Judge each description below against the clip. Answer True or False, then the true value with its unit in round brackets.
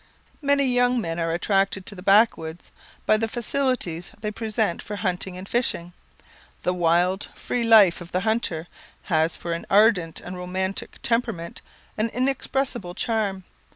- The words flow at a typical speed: True (150 wpm)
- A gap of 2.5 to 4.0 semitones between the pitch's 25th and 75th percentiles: False (4.6 semitones)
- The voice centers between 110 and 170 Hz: False (195 Hz)